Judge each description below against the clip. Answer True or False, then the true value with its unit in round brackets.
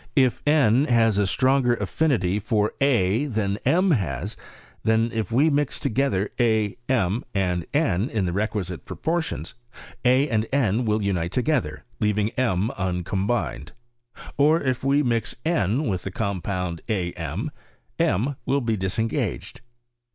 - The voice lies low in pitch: True (110 Hz)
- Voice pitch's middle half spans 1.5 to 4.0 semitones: False (5.4 semitones)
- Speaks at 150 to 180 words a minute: False (140 wpm)